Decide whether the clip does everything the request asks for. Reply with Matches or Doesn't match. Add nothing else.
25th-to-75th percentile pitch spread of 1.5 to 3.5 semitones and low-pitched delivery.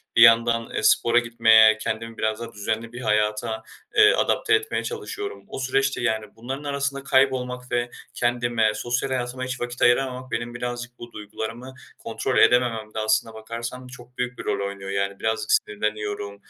Matches